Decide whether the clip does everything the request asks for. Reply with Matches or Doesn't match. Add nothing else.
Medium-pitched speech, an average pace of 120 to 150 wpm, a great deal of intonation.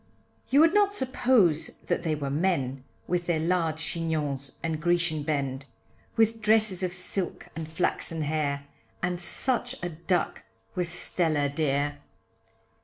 Doesn't match